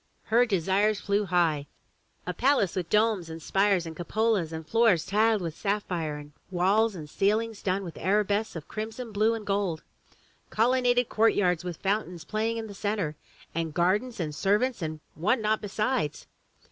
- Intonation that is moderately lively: Yes, average, 4.2 semitones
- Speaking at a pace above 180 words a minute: No, average, 170 wpm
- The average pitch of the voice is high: Yes, high, 200 Hz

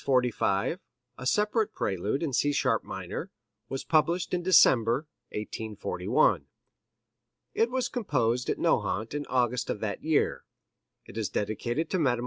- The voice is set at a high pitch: No, low, 130 Hz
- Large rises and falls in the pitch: Yes, wide, 6.5 semitones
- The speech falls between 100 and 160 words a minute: Yes, slow, 135 wpm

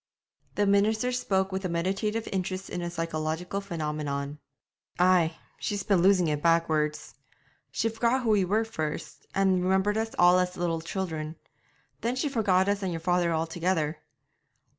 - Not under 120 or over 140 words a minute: No, average, 155 wpm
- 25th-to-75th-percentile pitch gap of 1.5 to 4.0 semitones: Yes, average, 3.4 semitones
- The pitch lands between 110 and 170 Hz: No, medium, 185 Hz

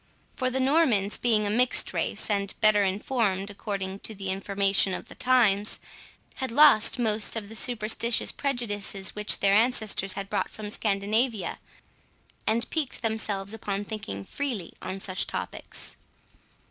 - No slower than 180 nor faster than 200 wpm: No, average, 145 wpm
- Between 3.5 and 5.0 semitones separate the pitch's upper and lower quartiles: No, average, 3.1 semitones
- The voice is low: No, high, 210 Hz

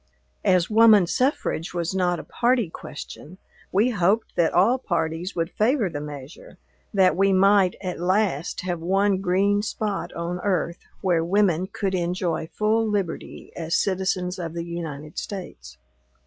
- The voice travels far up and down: No, average, 3.0 semitones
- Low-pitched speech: No, medium, 185 Hz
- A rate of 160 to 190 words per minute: No, average, 150 wpm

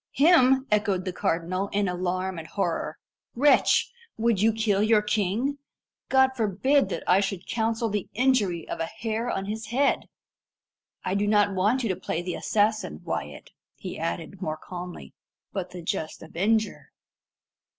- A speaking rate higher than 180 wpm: No, average, 155 wpm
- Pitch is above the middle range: Yes, high, 205 Hz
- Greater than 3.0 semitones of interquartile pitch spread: Yes, average, 3.8 semitones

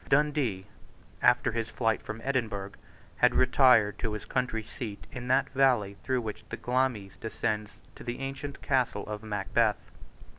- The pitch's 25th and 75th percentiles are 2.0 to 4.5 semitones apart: Yes, average, 3.5 semitones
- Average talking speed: Yes, average, 150 wpm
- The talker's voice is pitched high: No, low, 115 Hz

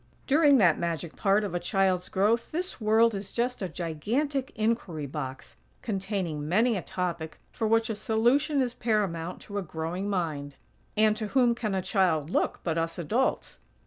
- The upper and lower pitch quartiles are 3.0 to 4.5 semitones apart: No, average, 5.2 semitones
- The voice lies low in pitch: No, high, 195 Hz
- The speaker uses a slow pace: No, average, 175 wpm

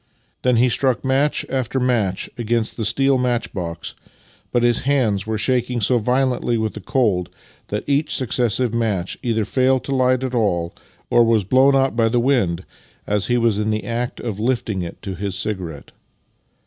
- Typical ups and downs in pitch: Yes, average, 3.5 semitones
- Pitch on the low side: Yes, low, 120 Hz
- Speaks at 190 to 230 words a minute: No, average, 180 wpm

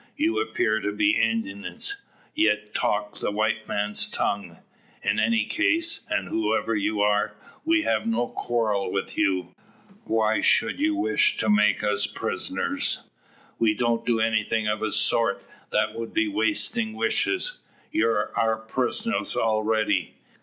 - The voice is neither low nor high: No, low, 110 Hz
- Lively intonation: Yes, wide, 7.1 semitones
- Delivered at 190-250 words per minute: No, average, 140 wpm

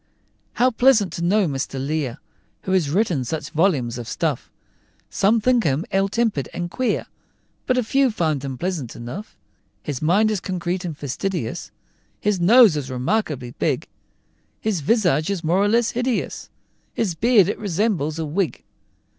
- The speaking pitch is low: No, medium, 180 Hz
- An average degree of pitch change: No, wide, 6.4 semitones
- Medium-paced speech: Yes, average, 160 wpm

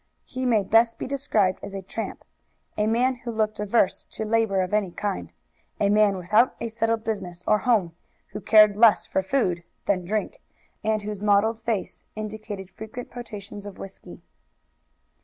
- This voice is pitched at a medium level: No, high, 215 Hz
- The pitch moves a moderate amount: No, narrow, 2.3 semitones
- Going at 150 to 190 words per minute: Yes, average, 165 wpm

